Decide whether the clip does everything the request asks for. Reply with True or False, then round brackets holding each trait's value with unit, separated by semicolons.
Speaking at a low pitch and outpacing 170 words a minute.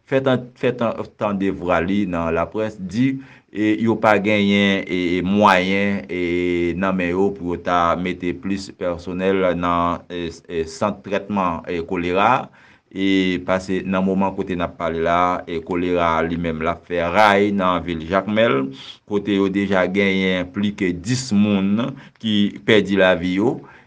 False (95 Hz; 155 wpm)